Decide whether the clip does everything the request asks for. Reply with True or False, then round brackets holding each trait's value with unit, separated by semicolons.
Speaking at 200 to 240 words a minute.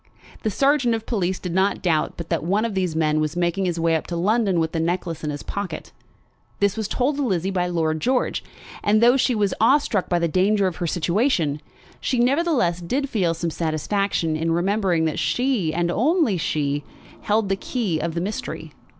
True (205 wpm)